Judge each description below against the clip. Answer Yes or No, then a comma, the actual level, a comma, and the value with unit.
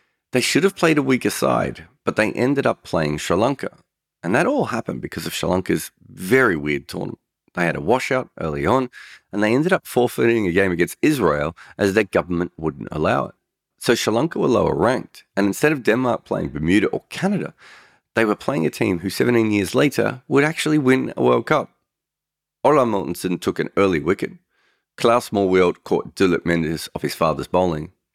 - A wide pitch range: Yes, wide, 6.5 semitones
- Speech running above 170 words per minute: Yes, average, 190 wpm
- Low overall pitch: Yes, low, 100 Hz